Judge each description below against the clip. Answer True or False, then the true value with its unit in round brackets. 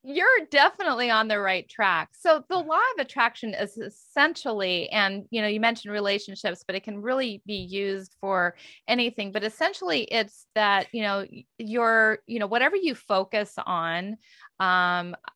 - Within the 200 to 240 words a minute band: False (160 wpm)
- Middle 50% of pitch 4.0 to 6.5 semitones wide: False (3.4 semitones)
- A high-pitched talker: True (215 Hz)